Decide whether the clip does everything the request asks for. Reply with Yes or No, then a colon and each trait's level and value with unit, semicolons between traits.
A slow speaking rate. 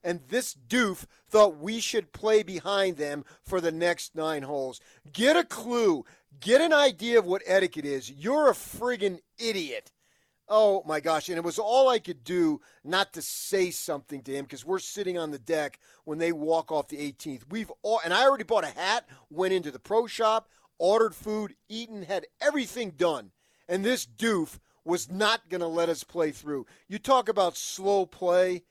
No: average, 190 wpm